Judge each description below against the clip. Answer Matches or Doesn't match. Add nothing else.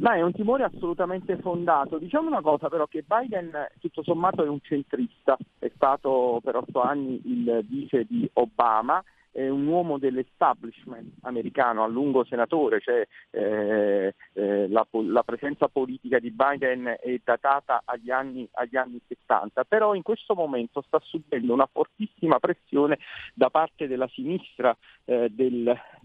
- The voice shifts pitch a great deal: Matches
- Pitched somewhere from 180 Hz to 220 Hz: Doesn't match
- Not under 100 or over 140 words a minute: Doesn't match